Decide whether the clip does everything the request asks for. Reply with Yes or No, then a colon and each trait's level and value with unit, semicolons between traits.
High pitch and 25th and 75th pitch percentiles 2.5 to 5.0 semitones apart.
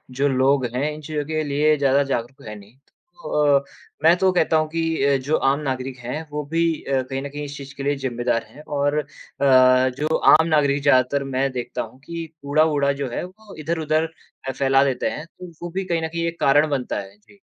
No: medium, 140 Hz; average, 2.9 semitones